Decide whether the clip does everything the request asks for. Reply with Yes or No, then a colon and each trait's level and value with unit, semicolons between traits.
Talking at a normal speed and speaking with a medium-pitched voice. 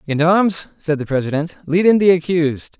Yes: average, 170 wpm; medium, 165 Hz